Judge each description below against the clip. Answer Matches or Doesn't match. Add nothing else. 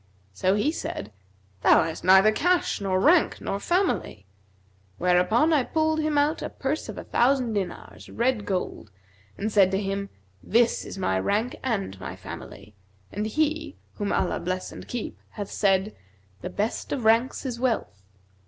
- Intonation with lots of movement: Matches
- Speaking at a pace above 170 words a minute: Doesn't match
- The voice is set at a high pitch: Matches